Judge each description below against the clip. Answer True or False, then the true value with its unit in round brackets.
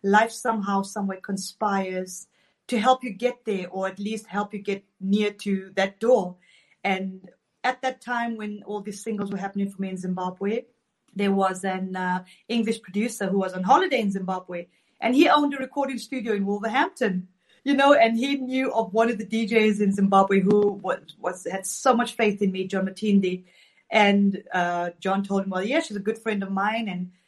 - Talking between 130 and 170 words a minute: False (200 wpm)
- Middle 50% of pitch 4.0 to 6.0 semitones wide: False (2.9 semitones)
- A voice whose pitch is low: False (205 Hz)